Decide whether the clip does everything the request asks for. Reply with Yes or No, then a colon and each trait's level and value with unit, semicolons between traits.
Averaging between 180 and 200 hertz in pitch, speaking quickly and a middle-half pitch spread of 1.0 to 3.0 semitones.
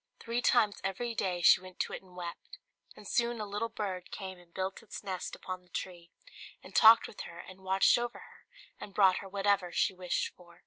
Yes: high, 190 Hz; fast, 215 wpm; narrow, 2.6 semitones